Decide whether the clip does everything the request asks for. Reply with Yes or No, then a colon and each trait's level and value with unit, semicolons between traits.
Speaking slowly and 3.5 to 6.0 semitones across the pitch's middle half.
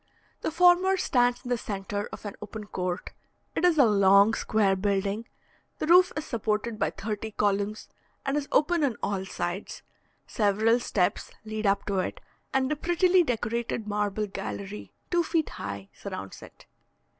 No: average, 160 wpm; wide, 5.5 semitones